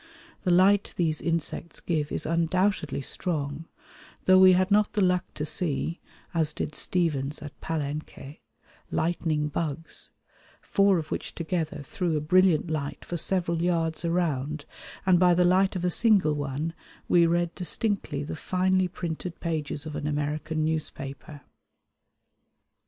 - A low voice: No, medium, 165 Hz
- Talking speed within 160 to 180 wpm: No, average, 140 wpm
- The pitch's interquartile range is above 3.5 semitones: No, average, 3.1 semitones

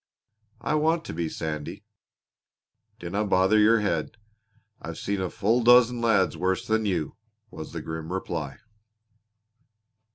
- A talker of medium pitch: No, very low, 95 Hz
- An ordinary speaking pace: No, slow, 130 wpm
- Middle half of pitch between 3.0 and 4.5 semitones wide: No, average, 5.2 semitones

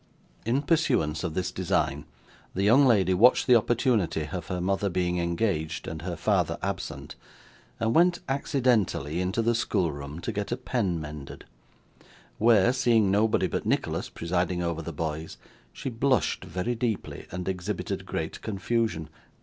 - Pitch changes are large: Yes, wide, 5.8 semitones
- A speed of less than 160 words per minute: Yes, average, 150 wpm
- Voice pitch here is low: Yes, very low, 95 Hz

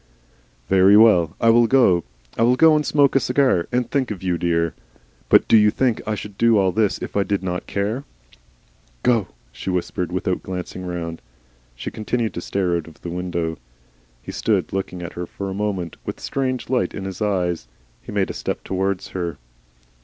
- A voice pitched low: Yes, very low, 95 Hz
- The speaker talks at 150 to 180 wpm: No, average, 200 wpm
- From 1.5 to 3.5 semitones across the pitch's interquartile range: No, average, 4.5 semitones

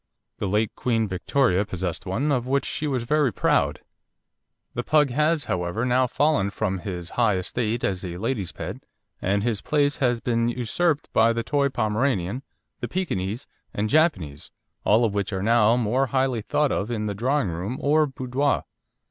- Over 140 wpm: Yes, average, 175 wpm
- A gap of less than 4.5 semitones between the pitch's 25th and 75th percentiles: No, average, 5.3 semitones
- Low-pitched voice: Yes, low, 115 Hz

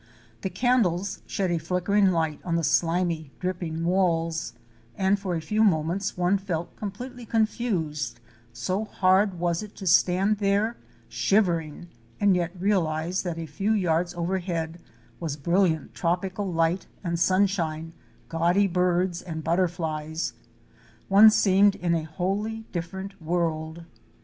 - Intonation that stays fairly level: No, average, 3.0 semitones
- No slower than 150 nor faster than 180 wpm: No, slow, 135 wpm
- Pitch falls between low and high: Yes, medium, 180 Hz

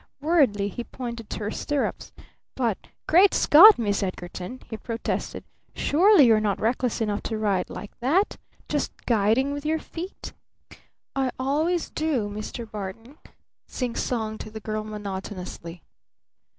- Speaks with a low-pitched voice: No, high, 230 Hz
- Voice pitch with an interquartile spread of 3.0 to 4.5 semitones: No, wide, 5.4 semitones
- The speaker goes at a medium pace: No, slow, 130 wpm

